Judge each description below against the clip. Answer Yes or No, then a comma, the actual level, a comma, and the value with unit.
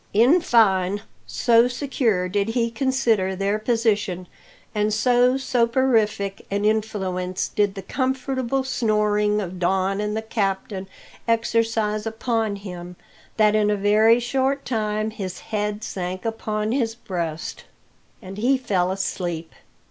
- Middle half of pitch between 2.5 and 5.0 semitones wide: Yes, average, 3.0 semitones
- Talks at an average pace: No, slow, 125 wpm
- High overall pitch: Yes, high, 215 Hz